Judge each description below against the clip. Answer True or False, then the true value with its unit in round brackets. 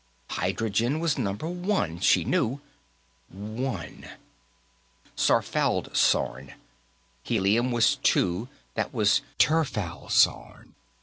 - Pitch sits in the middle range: False (115 Hz)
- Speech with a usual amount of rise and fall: False (6.5 semitones)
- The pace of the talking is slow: True (75 wpm)